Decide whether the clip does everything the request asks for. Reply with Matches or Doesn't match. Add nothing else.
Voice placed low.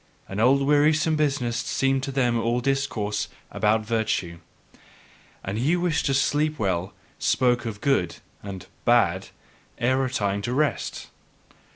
Matches